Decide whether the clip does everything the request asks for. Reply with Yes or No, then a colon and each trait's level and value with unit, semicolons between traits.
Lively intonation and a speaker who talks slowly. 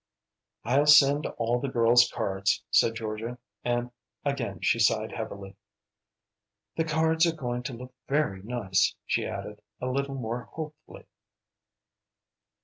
No: average, 4.1 semitones; slow, 130 wpm